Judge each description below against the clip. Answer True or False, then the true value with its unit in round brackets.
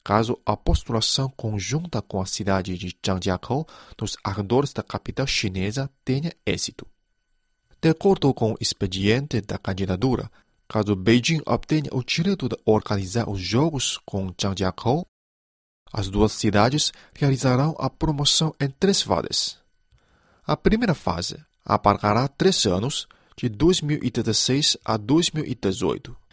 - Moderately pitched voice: False (115 Hz)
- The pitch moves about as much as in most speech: False (5.7 semitones)